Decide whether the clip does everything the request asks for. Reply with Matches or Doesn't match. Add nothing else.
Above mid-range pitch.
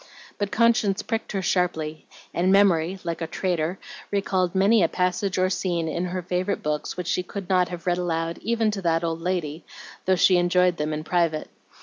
Doesn't match